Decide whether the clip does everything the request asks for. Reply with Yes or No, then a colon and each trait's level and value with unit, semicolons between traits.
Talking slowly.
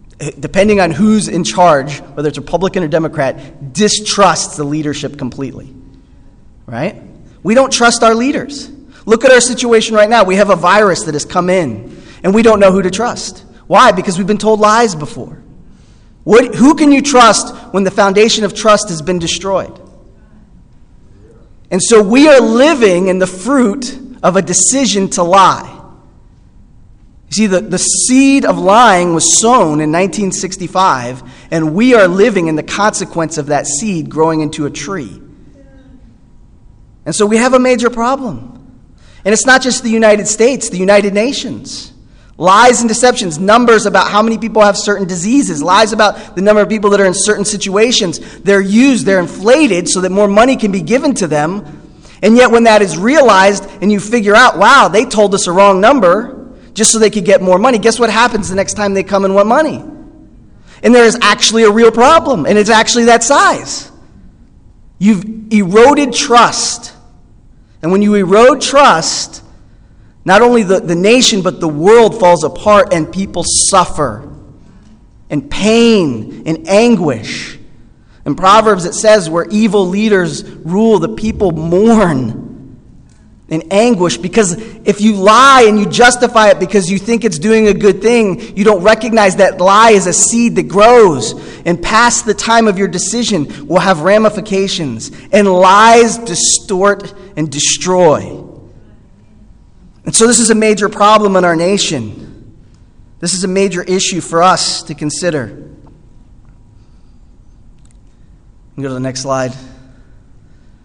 No: average, 160 wpm